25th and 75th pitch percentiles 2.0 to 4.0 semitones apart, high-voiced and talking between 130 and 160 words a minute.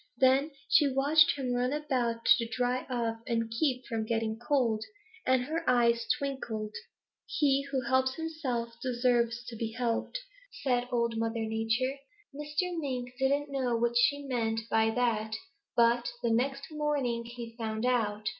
Yes: average, 3.0 semitones; high, 245 Hz; average, 150 wpm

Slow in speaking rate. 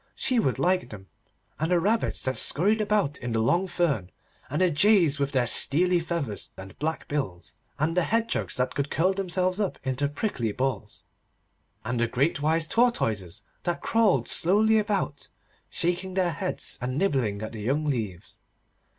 No: average, 165 wpm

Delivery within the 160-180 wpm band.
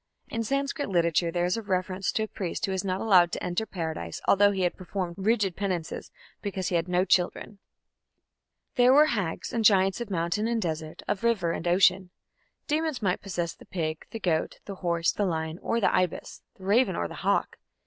No: average, 200 wpm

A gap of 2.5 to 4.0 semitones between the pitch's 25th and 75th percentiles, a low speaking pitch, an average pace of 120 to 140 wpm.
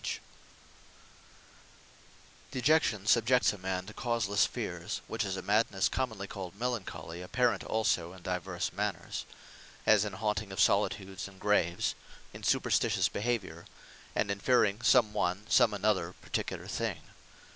Yes: average, 2.9 semitones; low, 100 Hz; slow, 135 wpm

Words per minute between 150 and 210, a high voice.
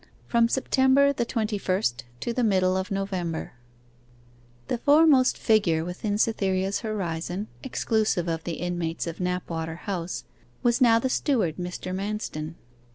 No: slow, 135 wpm; high, 195 Hz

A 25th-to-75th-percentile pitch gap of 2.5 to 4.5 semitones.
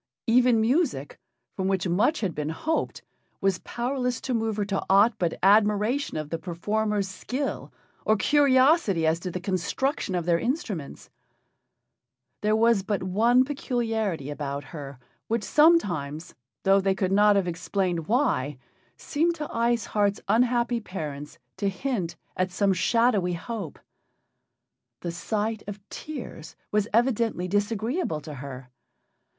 No: average, 5.2 semitones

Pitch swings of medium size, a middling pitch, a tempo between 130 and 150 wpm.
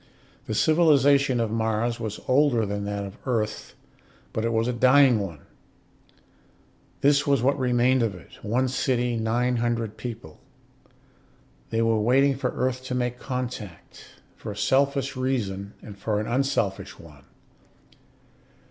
No: average, 3.3 semitones; low, 120 Hz; average, 140 wpm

